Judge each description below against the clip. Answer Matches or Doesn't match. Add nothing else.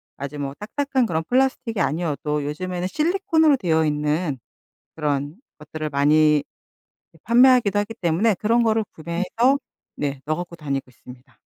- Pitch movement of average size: Doesn't match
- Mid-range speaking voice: Matches